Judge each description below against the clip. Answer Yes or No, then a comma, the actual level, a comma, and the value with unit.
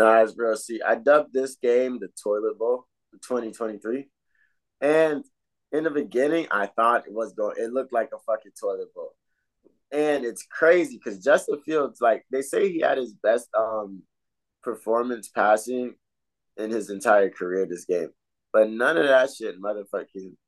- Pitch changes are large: Yes, wide, 6.9 semitones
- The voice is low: Yes, low, 125 Hz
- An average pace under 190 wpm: Yes, average, 165 wpm